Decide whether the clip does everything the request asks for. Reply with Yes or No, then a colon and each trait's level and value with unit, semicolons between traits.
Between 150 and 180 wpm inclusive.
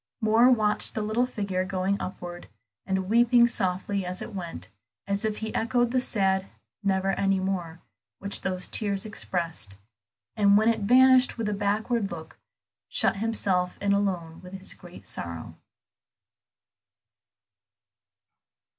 No: slow, 135 wpm